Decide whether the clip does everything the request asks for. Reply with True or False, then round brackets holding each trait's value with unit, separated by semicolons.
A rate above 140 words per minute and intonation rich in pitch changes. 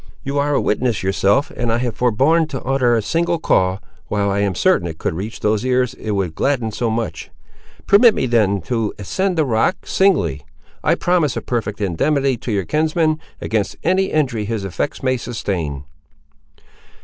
True (180 wpm; 6.0 semitones)